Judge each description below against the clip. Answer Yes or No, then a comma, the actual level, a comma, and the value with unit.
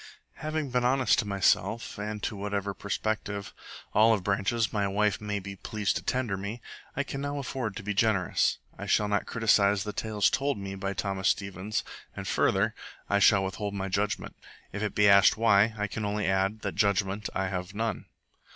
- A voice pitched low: Yes, low, 105 Hz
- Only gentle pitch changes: Yes, narrow, 1.9 semitones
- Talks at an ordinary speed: Yes, average, 190 wpm